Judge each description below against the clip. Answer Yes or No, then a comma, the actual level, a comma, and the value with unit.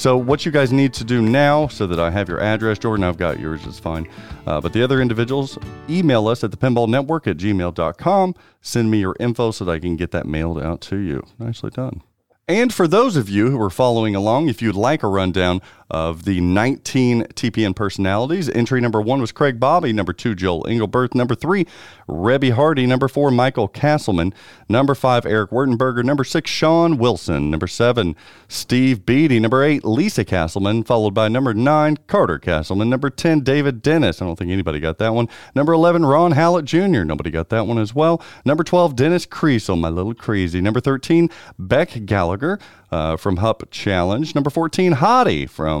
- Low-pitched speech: Yes, low, 115 Hz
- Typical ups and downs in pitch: No, wide, 6.5 semitones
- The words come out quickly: No, average, 195 wpm